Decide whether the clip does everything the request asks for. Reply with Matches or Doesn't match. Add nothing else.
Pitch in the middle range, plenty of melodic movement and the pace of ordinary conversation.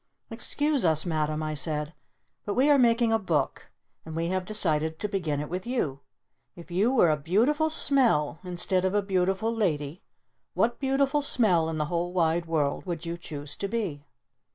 Matches